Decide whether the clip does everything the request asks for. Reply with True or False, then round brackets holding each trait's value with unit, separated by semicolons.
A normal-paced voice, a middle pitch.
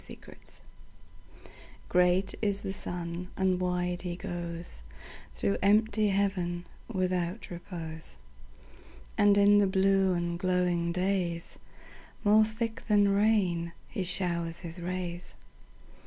False (100 wpm; 180 Hz)